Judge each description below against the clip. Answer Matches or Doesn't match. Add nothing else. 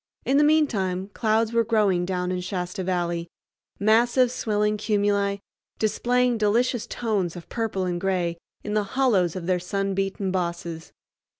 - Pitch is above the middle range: Matches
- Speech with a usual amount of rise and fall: Matches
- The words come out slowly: Doesn't match